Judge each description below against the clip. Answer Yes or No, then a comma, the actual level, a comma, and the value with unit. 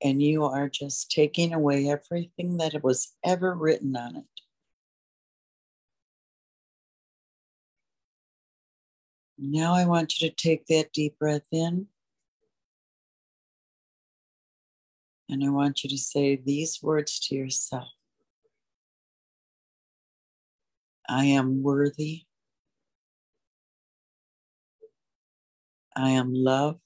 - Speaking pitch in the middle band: Yes, medium, 150 Hz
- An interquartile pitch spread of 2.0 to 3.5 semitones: Yes, average, 2.8 semitones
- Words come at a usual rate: No, slow, 85 wpm